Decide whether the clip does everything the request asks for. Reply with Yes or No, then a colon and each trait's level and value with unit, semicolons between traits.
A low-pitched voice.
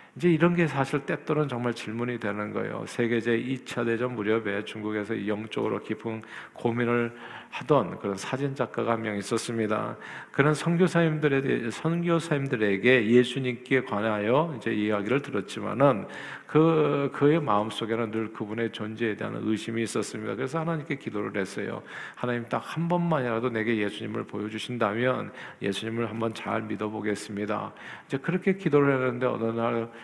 Yes: low, 115 Hz